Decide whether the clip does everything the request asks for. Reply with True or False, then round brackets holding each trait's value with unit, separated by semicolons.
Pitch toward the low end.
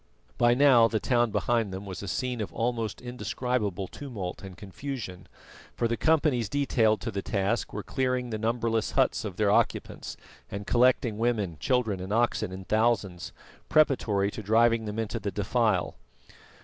True (115 Hz)